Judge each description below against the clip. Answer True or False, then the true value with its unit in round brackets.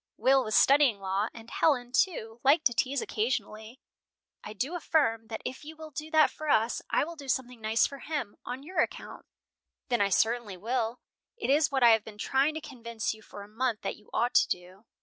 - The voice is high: True (245 Hz)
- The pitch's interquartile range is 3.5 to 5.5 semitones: True (4.4 semitones)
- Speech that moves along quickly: True (215 wpm)